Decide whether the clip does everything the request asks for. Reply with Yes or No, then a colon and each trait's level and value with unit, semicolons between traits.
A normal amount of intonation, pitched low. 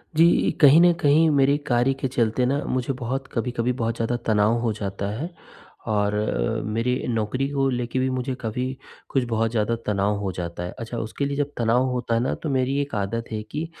Yes: average, 3.6 semitones; low, 120 Hz